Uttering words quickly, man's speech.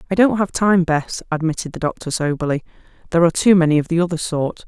No: fast, 220 wpm; female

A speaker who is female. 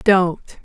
Yes: female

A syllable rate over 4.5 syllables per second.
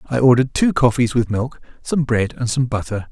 Yes: 5.5 syllables/s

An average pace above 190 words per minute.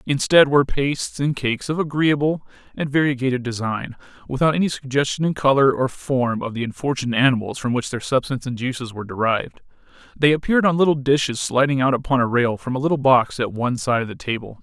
Yes: average, 200 wpm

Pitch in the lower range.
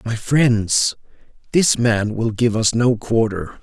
Yes: low, 115 Hz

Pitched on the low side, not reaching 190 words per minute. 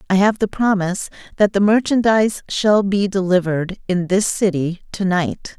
No: high, 195 Hz; average, 160 wpm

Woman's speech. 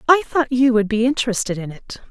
Yes: female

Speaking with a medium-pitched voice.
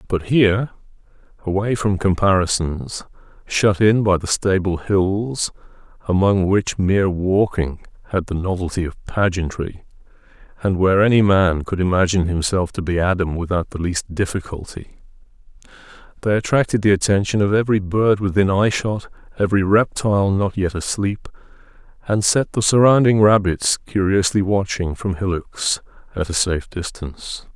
No: very low, 95 Hz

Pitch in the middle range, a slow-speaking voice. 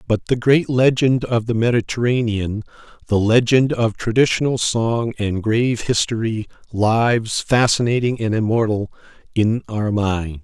No: low, 115 Hz; slow, 125 wpm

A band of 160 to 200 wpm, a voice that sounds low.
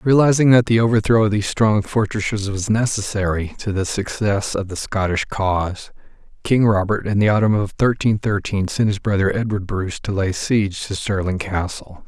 Yes: average, 180 wpm; low, 100 Hz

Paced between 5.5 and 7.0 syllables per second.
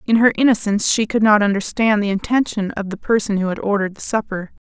Yes: 6.3 syllables/s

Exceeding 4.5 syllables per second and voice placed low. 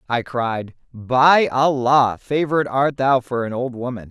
No: 4.0 syllables/s; low, 130 Hz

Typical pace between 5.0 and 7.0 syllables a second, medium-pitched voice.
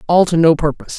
No: 7.2 syllables/s; medium, 165 Hz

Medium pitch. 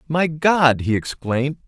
Yes: medium, 145 Hz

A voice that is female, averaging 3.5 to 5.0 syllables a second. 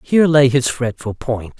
No: male; 4.8 syllables/s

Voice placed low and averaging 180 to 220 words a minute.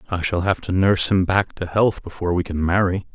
No: very low, 95 Hz; fast, 250 wpm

